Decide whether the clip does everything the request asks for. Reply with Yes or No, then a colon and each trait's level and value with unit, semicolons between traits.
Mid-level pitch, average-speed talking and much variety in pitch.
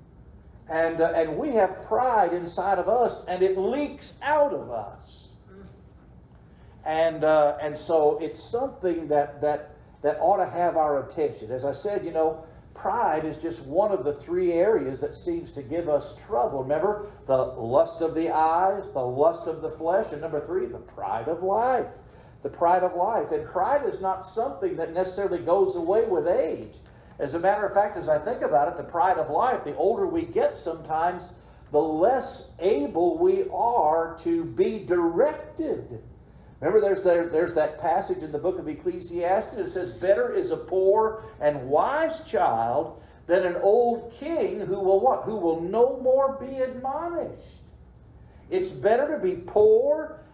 Yes: medium, 175 Hz; average, 175 wpm; wide, 7.0 semitones